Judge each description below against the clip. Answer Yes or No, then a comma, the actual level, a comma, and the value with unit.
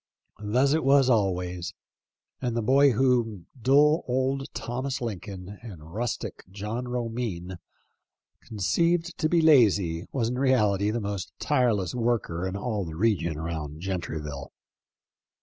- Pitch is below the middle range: Yes, low, 110 Hz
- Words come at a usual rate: No, slow, 130 wpm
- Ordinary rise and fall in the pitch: No, wide, 5.9 semitones